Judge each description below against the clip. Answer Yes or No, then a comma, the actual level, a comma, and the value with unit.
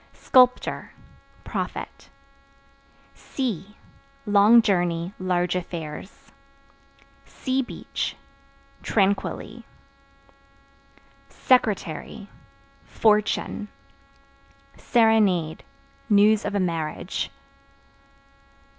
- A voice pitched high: Yes, high, 200 Hz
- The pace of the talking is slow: Yes, slow, 50 wpm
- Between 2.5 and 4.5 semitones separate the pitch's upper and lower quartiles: Yes, average, 3.9 semitones